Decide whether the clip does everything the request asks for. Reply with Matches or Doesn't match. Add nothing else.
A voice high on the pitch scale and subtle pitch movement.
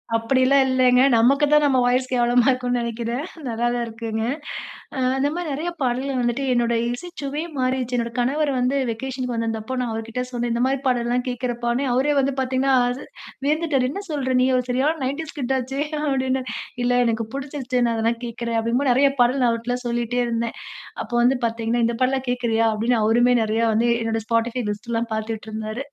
Matches